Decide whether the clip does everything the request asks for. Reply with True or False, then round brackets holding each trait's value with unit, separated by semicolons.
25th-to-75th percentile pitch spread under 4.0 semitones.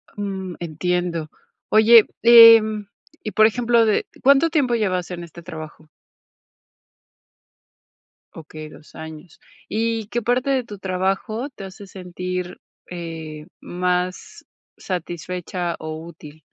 False (4.6 semitones)